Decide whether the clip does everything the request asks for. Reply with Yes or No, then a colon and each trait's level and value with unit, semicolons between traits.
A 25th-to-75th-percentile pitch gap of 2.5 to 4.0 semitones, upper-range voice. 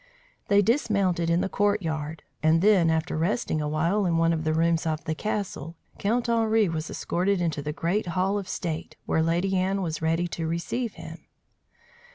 No: average, 3.7 semitones; medium, 170 Hz